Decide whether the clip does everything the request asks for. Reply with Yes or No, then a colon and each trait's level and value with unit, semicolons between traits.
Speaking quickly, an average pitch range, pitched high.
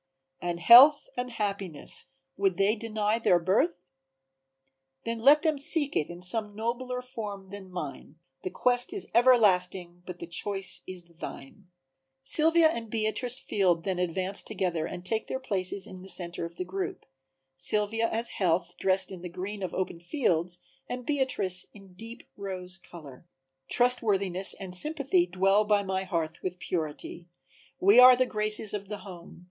No: average, 160 wpm; average, 4.1 semitones; high, 195 Hz